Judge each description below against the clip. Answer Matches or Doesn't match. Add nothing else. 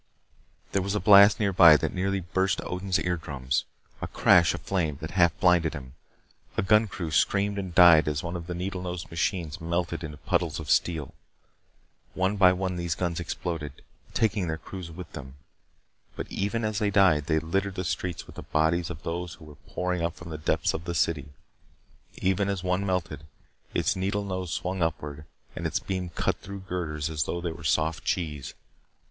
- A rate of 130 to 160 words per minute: Doesn't match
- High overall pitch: Doesn't match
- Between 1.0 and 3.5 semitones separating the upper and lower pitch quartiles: Matches